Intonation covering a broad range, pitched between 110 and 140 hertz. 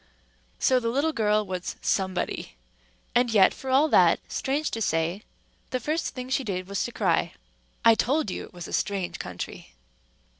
No: wide, 5.8 semitones; high, 220 Hz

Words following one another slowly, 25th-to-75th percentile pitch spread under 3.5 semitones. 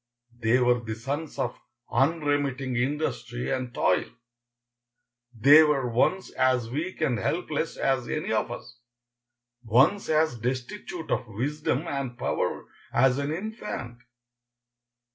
No: slow, 120 wpm; average, 3.9 semitones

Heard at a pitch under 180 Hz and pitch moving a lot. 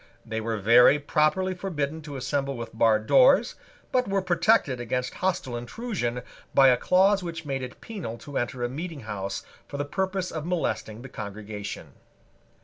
Yes: medium, 140 Hz; wide, 7.4 semitones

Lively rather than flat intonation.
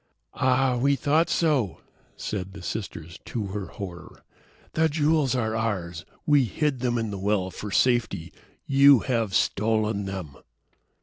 Yes: wide, 5.7 semitones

